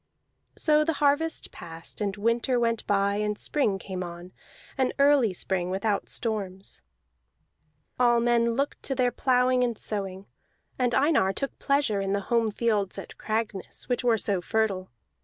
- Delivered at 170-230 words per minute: No, average, 155 wpm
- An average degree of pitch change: Yes, average, 4.2 semitones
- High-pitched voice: Yes, high, 225 Hz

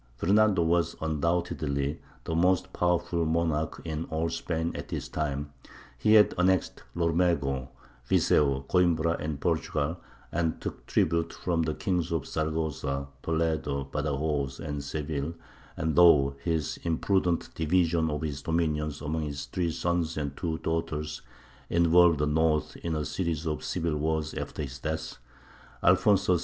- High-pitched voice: No, very low, 80 Hz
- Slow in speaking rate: No, average, 145 wpm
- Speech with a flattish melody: Yes, narrow, 2.2 semitones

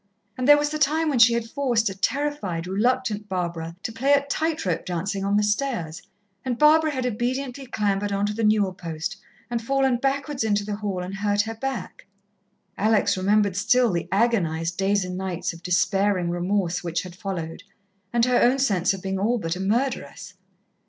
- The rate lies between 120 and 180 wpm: No, average, 190 wpm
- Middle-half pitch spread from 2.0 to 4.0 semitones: No, average, 5.2 semitones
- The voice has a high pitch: Yes, high, 205 Hz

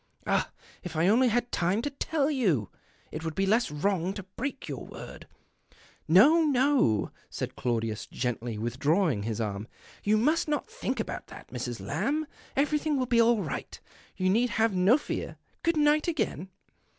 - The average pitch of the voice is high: Yes, high, 210 Hz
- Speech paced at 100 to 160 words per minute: No, average, 180 wpm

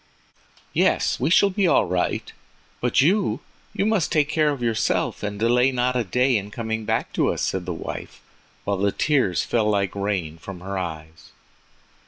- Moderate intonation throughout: No, wide, 5.8 semitones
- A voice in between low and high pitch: No, low, 110 Hz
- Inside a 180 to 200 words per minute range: No, average, 170 wpm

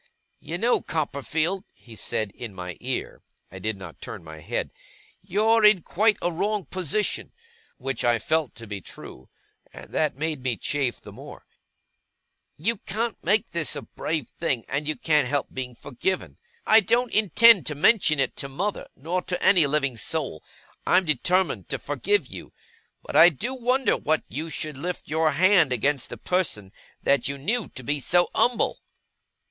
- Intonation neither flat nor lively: No, wide, 6.3 semitones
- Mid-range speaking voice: Yes, medium, 155 Hz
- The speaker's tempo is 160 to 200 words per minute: Yes, average, 170 wpm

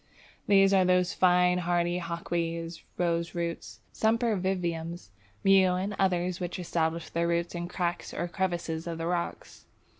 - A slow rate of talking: Yes, slow, 130 wpm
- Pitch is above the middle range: No, medium, 175 Hz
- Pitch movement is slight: Yes, narrow, 1.4 semitones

